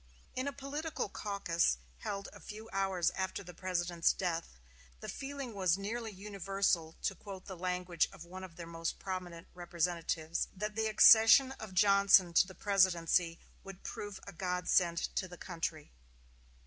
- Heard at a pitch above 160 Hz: Yes, medium, 185 Hz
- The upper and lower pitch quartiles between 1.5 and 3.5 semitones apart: Yes, average, 2.8 semitones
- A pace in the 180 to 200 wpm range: No, average, 155 wpm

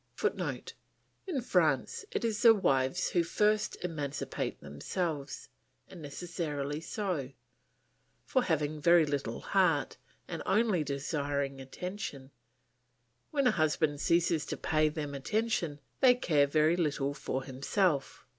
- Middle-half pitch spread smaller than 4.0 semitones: No, average, 4.4 semitones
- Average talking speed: No, slow, 120 wpm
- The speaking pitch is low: No, medium, 155 Hz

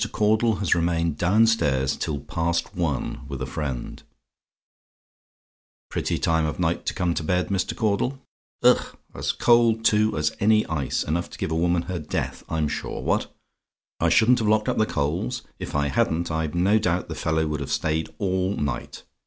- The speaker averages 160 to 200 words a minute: Yes, average, 180 wpm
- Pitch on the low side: Yes, very low, 85 Hz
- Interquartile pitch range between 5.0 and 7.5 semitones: Yes, average, 5.3 semitones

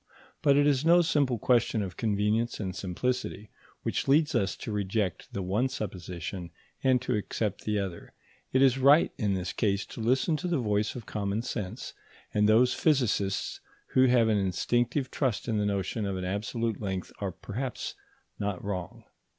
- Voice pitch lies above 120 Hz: No, low, 105 Hz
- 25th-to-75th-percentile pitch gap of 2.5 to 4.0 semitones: No, average, 4.4 semitones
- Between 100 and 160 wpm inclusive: No, average, 175 wpm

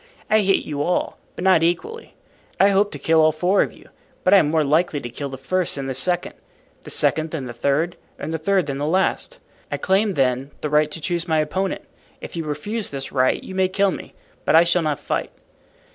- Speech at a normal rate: No, fast, 230 wpm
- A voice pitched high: No, medium, 160 Hz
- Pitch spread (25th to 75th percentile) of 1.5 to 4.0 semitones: No, average, 4.5 semitones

